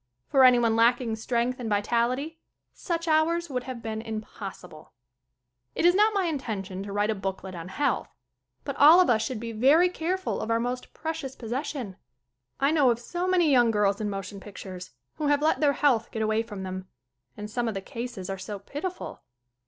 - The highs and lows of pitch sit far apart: Yes, wide, 5.9 semitones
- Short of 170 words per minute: No, average, 190 wpm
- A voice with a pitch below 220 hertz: No, high, 235 Hz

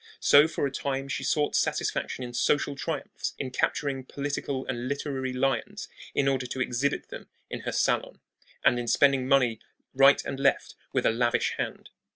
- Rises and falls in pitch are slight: Yes, narrow, 1.7 semitones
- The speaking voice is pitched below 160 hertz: Yes, low, 135 Hz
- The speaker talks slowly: No, average, 175 wpm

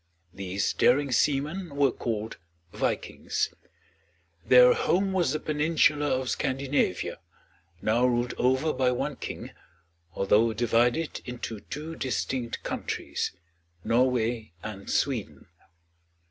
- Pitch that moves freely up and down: No, average, 4.0 semitones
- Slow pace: Yes, slow, 105 wpm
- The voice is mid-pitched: No, low, 125 Hz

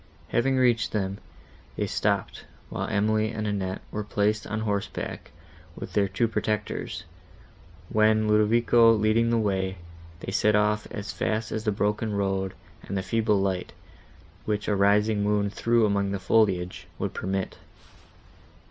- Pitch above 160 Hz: No, low, 105 Hz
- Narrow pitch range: Yes, narrow, 1.6 semitones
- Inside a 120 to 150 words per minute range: Yes, average, 145 wpm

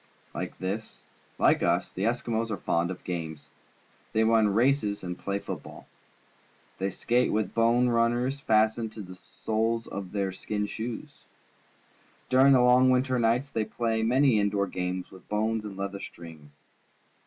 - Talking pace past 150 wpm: Yes, average, 160 wpm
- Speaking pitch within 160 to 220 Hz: No, low, 110 Hz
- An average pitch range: Yes, average, 3.3 semitones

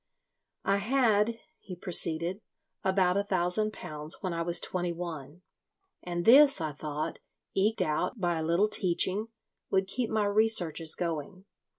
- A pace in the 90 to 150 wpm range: Yes, average, 145 wpm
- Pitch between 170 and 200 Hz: Yes, medium, 185 Hz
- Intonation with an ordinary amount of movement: Yes, average, 3.8 semitones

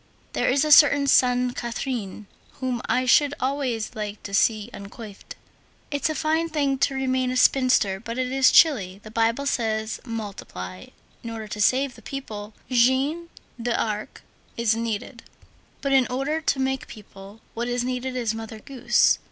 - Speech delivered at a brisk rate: No, average, 160 wpm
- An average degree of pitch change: Yes, average, 3.6 semitones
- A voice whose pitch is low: No, high, 245 Hz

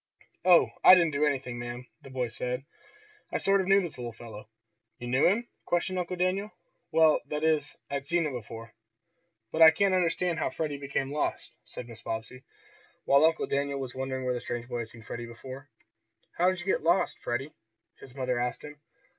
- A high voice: No, medium, 140 Hz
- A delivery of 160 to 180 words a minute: No, average, 195 wpm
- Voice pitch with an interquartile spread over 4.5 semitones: Yes, average, 5.3 semitones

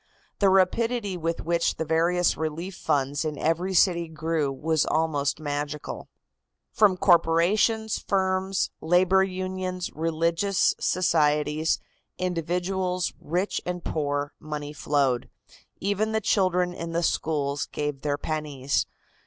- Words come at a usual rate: No, slow, 115 wpm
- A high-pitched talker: No, medium, 165 Hz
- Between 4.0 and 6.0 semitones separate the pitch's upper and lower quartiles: No, average, 3.6 semitones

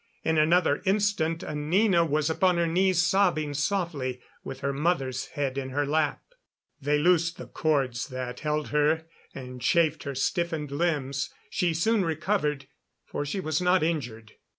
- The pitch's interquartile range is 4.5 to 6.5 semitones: No, average, 3.7 semitones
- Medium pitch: Yes, medium, 155 Hz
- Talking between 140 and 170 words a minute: Yes, average, 150 wpm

